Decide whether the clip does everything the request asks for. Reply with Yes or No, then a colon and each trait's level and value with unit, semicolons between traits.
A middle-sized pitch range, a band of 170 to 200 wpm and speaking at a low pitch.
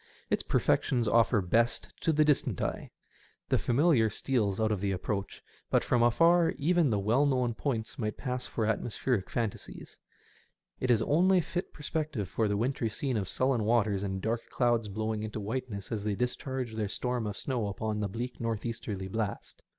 Yes: average, 3.4 semitones; average, 180 wpm; low, 115 Hz